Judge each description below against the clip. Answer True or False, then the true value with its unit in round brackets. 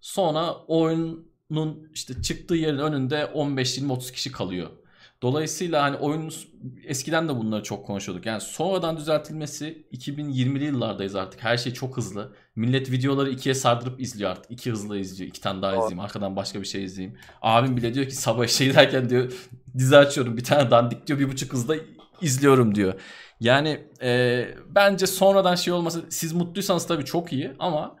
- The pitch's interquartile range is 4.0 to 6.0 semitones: True (4.8 semitones)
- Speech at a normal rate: False (165 wpm)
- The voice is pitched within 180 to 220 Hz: False (135 Hz)